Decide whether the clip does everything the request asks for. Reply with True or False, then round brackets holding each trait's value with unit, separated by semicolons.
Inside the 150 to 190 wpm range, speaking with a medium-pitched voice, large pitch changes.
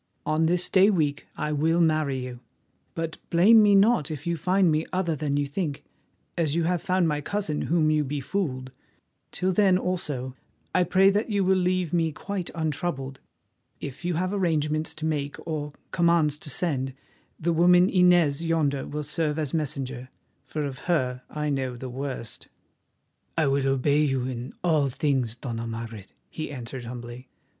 False (170 wpm; 155 Hz; 4.3 semitones)